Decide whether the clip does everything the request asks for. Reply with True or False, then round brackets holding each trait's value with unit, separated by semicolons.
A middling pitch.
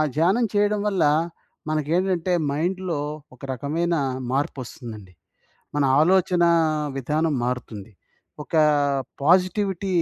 True (165 Hz)